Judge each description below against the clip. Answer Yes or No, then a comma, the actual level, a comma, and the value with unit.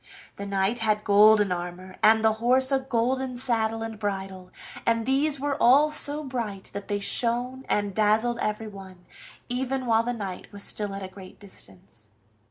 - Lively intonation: No, average, 3.9 semitones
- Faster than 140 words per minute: Yes, average, 170 wpm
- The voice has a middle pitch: No, high, 220 Hz